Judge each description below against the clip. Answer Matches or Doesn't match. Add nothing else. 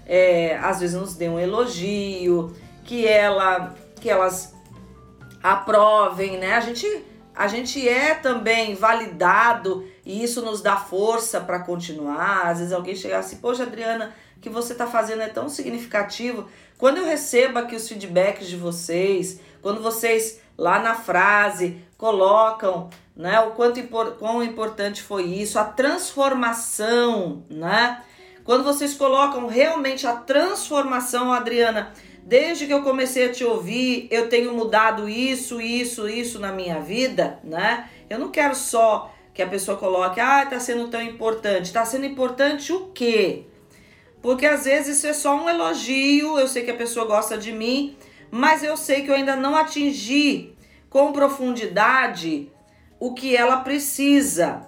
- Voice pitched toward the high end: Matches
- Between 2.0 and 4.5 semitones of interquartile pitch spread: Doesn't match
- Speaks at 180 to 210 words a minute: Doesn't match